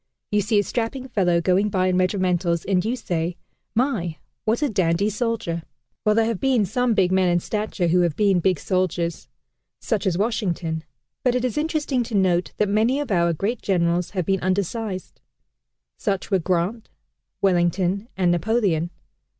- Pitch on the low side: No, high, 190 Hz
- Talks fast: No, average, 170 wpm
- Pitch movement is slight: No, average, 4.1 semitones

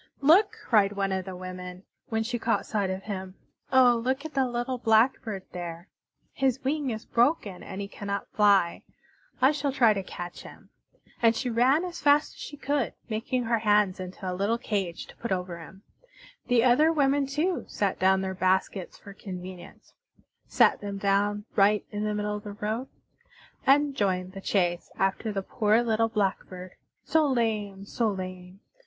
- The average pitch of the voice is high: Yes, high, 210 Hz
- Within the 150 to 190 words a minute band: Yes, average, 175 wpm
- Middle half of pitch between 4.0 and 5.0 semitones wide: Yes, average, 4.6 semitones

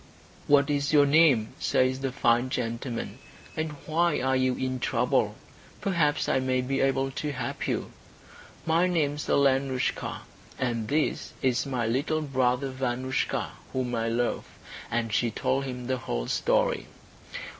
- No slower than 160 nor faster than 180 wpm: No, average, 145 wpm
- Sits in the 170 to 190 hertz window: No, low, 130 Hz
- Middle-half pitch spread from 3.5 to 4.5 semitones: No, narrow, 2.5 semitones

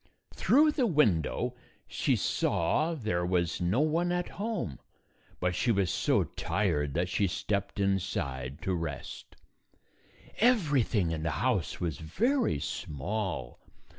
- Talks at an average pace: No, slow, 125 wpm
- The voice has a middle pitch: No, very low, 95 Hz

